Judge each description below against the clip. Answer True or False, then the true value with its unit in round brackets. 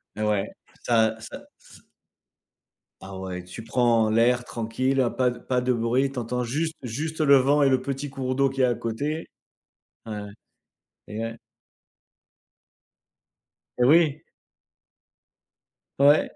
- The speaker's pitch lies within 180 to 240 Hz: False (125 Hz)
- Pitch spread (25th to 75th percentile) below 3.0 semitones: False (3.3 semitones)